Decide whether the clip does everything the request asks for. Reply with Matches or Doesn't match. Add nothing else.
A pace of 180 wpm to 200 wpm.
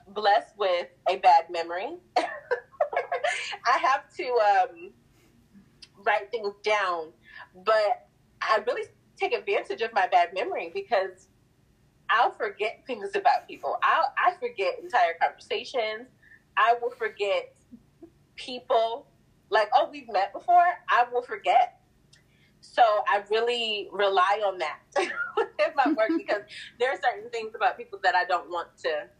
Doesn't match